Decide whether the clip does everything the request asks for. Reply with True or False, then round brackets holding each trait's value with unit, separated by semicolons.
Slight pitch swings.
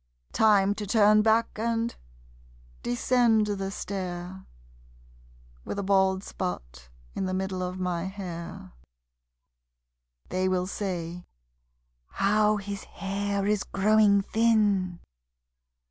True (2.3 semitones)